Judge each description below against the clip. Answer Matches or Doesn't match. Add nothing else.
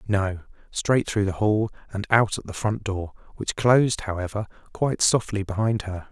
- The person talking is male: Matches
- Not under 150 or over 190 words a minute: Matches